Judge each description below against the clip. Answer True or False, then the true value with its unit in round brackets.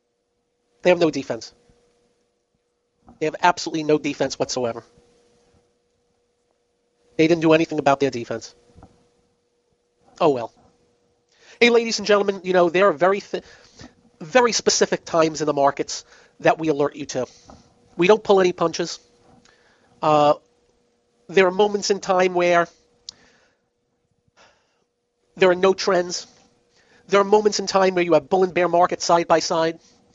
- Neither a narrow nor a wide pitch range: True (4.0 semitones)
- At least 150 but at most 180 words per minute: False (140 wpm)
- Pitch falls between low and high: True (175 Hz)